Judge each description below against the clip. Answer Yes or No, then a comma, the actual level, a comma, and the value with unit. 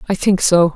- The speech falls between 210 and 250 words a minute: Yes, fast, 240 wpm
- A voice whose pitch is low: No, medium, 185 Hz